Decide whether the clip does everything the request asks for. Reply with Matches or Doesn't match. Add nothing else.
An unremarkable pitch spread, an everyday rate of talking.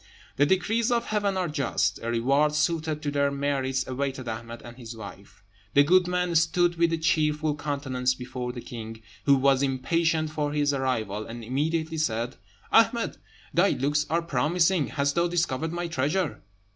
Matches